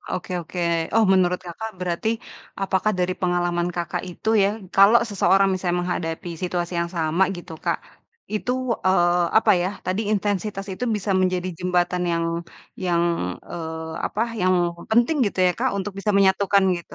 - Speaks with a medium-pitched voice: Yes, medium, 180 Hz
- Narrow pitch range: Yes, narrow, 2.1 semitones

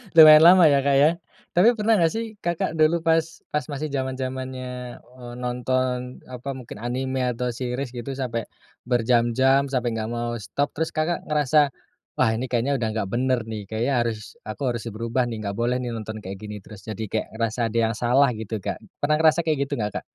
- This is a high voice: No, low, 125 Hz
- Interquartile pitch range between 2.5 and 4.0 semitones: Yes, average, 3.5 semitones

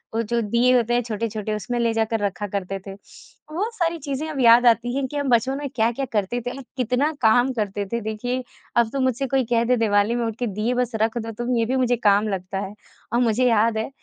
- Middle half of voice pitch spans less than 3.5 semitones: Yes, narrow, 2.5 semitones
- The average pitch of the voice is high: Yes, high, 235 Hz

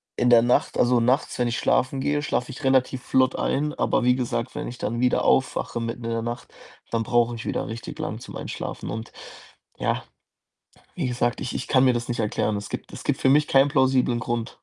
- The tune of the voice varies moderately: No, narrow, 2.0 semitones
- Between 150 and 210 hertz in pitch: No, low, 125 Hz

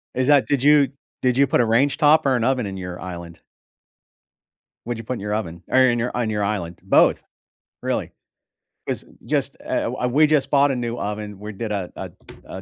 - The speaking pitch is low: Yes, low, 120 Hz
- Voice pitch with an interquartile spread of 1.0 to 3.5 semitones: No, average, 4.7 semitones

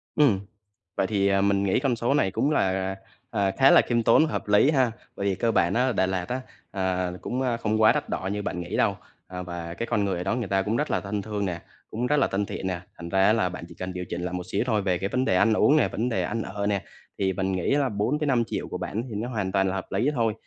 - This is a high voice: No, low, 100 Hz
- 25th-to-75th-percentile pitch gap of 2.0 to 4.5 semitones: Yes, average, 3.8 semitones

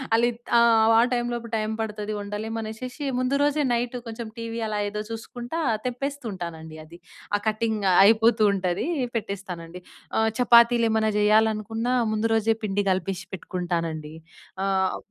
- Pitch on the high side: Yes, high, 220 Hz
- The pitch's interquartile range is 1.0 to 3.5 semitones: Yes, average, 3.0 semitones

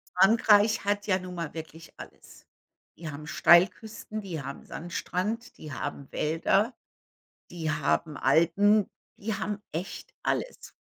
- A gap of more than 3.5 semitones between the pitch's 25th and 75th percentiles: Yes, average, 4.4 semitones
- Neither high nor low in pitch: Yes, medium, 180 Hz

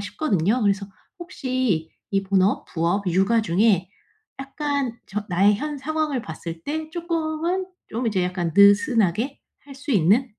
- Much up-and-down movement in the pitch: Yes, wide, 6.9 semitones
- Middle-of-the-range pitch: No, high, 220 Hz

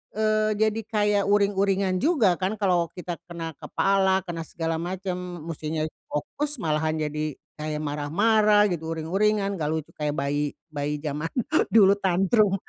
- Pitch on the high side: No, medium, 180 Hz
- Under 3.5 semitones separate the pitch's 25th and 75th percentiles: No, average, 4.7 semitones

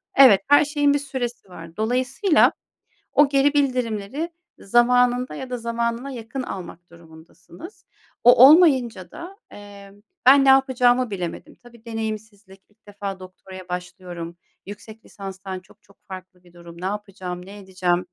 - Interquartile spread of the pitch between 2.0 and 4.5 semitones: No, wide, 5.4 semitones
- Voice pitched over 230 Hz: No, high, 220 Hz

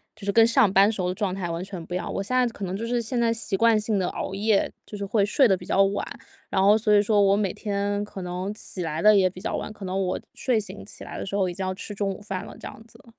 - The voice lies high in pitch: Yes, high, 200 Hz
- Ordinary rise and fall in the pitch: No, narrow, 2.2 semitones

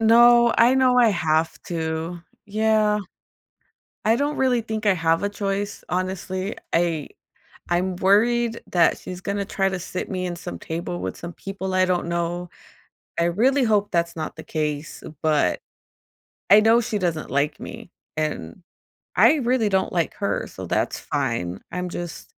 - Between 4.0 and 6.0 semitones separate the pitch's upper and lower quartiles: Yes, average, 4.5 semitones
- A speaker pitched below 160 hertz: No, medium, 185 Hz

